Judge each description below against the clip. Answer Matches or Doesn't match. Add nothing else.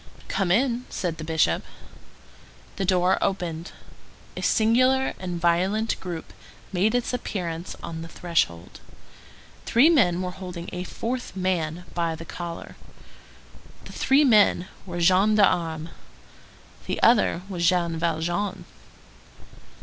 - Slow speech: Matches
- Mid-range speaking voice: Matches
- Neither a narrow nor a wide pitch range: Matches